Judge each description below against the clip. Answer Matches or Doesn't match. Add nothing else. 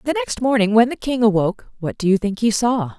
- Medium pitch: Doesn't match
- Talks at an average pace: Doesn't match